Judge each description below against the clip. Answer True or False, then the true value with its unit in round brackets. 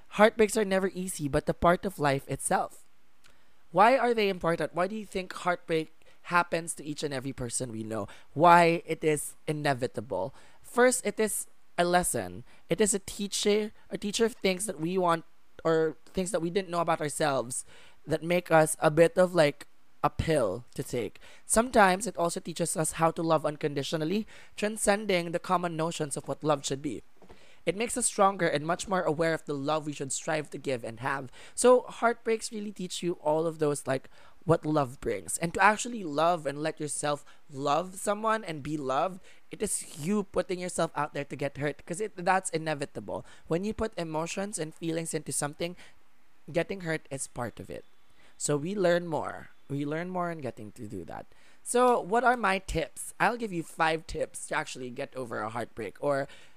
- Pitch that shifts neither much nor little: True (4.5 semitones)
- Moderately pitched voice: True (165 Hz)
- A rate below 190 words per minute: False (195 wpm)